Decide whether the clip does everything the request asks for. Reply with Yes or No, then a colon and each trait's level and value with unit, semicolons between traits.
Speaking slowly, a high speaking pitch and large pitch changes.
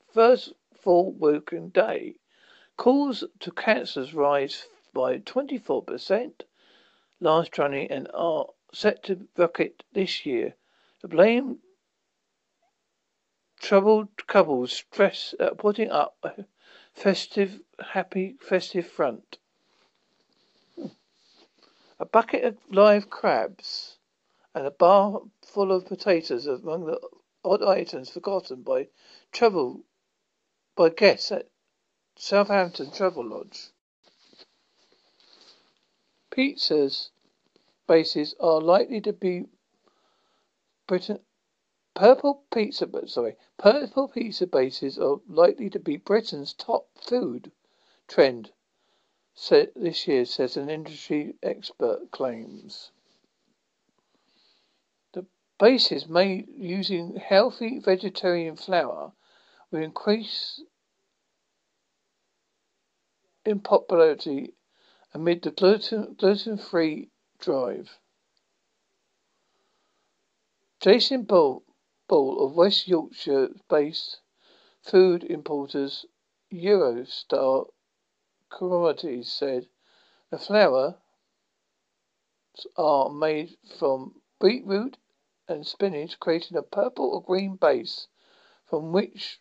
Yes: slow, 85 wpm; high, 205 Hz; wide, 8.7 semitones